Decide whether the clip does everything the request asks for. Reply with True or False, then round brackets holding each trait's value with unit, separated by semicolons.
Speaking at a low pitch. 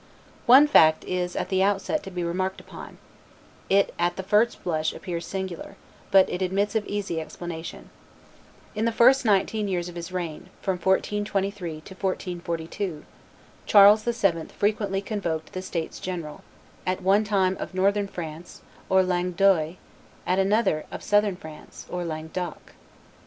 False (190 Hz)